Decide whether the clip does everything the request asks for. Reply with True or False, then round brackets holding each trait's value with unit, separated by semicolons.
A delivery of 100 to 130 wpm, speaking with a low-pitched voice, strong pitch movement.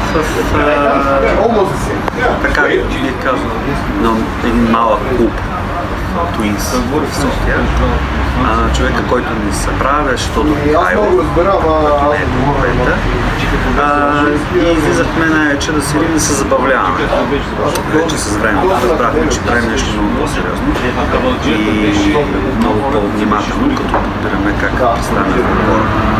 True (120 wpm; 115 Hz; 6.1 semitones)